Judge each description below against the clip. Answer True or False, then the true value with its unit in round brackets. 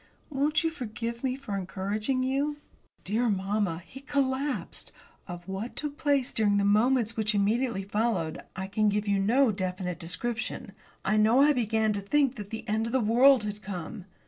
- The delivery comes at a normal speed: True (175 wpm)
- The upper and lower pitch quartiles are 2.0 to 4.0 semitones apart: False (4.5 semitones)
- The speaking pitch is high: True (220 Hz)